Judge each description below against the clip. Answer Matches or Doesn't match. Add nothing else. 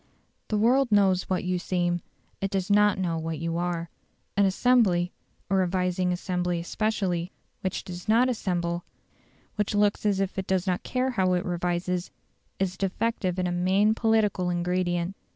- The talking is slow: Doesn't match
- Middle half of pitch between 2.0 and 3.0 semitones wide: Matches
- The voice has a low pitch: Doesn't match